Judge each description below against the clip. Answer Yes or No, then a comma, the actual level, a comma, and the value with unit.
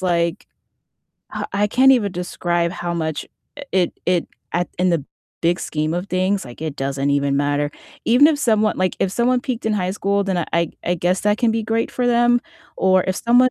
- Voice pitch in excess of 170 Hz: Yes, medium, 185 Hz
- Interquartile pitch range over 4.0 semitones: Yes, average, 4.7 semitones